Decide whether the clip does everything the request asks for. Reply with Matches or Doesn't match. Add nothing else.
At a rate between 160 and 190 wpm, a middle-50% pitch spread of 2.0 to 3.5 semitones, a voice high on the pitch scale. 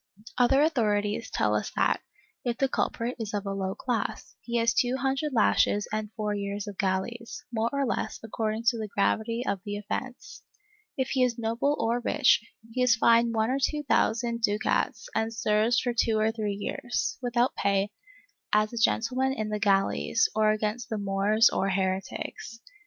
Matches